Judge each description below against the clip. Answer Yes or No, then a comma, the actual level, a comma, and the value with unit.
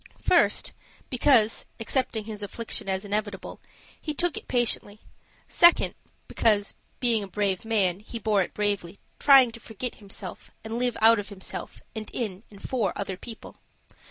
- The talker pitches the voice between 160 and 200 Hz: No, high, 215 Hz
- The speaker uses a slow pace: No, average, 155 wpm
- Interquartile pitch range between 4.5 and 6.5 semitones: No, average, 2.7 semitones